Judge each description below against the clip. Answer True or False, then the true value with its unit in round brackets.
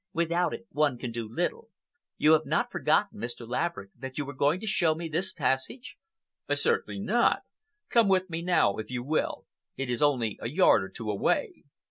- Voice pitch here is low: False (145 Hz)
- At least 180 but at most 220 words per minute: True (190 wpm)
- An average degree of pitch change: False (5.9 semitones)